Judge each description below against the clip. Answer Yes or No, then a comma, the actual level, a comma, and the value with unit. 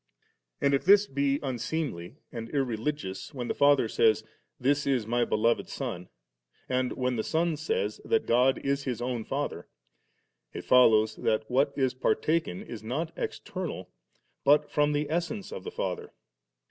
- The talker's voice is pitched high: No, low, 130 Hz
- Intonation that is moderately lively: Yes, average, 4.2 semitones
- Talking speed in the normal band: Yes, average, 155 wpm